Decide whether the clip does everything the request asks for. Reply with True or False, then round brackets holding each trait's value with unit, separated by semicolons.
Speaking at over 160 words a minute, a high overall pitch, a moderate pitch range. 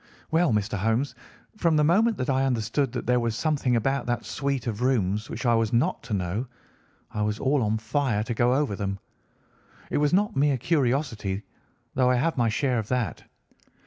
False (195 wpm; 125 Hz; 4.2 semitones)